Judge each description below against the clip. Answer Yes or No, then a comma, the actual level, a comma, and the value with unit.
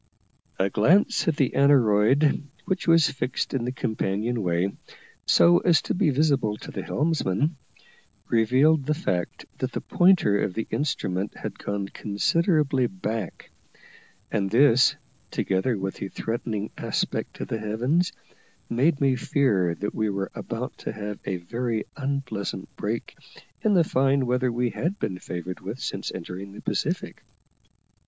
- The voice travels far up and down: Yes, wide, 5.8 semitones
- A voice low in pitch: Yes, low, 120 Hz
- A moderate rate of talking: Yes, average, 145 wpm